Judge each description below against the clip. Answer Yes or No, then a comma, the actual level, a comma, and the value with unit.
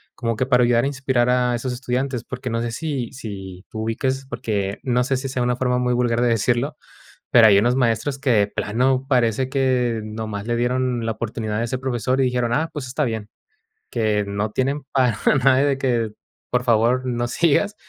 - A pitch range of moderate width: No, narrow, 2.3 semitones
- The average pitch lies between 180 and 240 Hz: No, low, 125 Hz